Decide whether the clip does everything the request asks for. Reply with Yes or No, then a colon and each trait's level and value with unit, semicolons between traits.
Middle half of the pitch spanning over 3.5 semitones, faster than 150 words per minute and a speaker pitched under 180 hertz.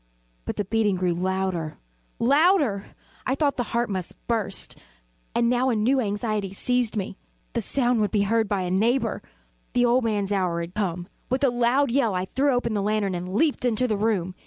No: average, 4.2 semitones; average, 195 wpm; high, 215 Hz